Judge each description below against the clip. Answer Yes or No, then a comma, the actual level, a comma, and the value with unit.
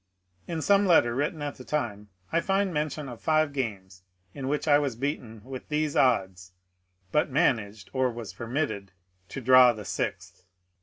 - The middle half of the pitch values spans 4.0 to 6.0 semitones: Yes, average, 5.3 semitones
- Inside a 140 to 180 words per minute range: Yes, average, 165 wpm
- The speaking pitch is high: No, low, 130 Hz